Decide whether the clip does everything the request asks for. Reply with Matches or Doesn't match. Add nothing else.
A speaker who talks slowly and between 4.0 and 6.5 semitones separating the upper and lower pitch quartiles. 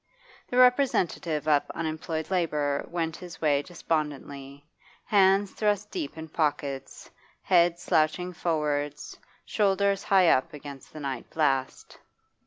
Matches